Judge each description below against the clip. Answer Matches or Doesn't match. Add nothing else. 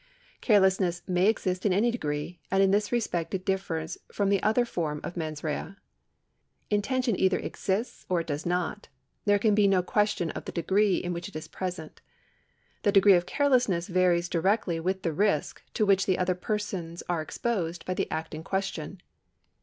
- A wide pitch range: Doesn't match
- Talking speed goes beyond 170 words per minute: Matches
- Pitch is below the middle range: Doesn't match